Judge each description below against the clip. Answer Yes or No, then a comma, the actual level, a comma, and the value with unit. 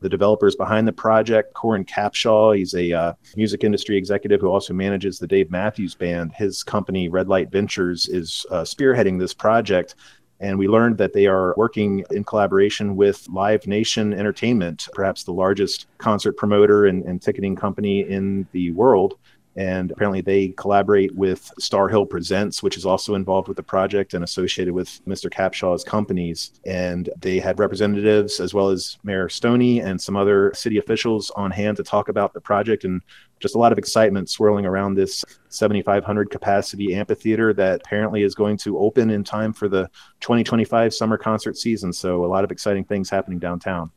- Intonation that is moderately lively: No, narrow, 2.1 semitones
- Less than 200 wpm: Yes, average, 180 wpm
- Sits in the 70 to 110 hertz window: Yes, low, 100 Hz